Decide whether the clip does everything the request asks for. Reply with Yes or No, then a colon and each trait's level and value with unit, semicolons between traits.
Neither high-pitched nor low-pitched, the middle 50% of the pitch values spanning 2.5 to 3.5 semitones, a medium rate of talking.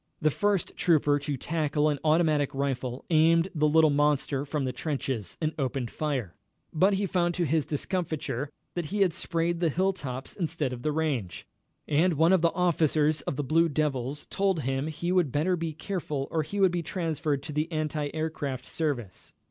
Yes: medium, 155 Hz; average, 3.0 semitones; average, 185 wpm